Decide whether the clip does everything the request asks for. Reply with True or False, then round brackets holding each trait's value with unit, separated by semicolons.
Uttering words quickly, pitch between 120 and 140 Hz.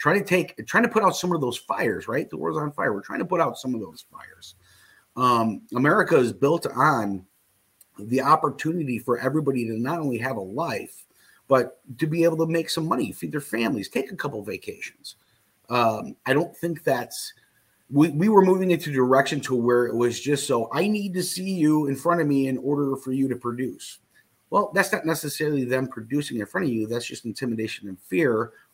True (215 wpm; 135 Hz)